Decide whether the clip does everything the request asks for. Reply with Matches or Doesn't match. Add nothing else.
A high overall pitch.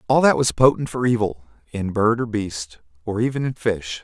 Doesn't match